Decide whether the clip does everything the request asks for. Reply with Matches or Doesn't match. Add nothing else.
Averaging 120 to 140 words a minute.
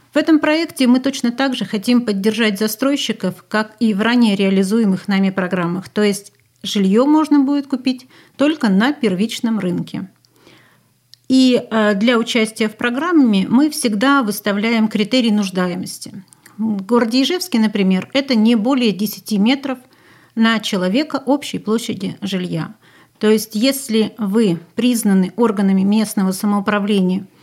Matches